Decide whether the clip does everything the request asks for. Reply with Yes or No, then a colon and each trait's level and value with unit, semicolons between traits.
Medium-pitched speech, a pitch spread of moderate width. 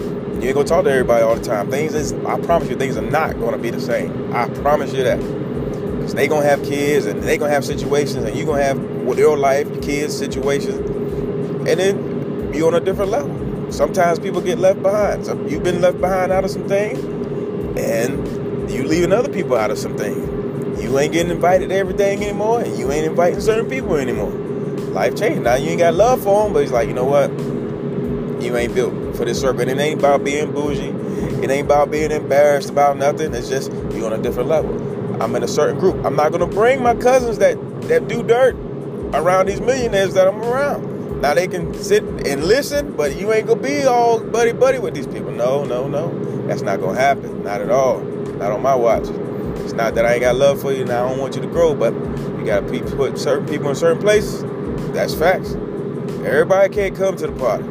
No: medium, 175 Hz; wide, 6.7 semitones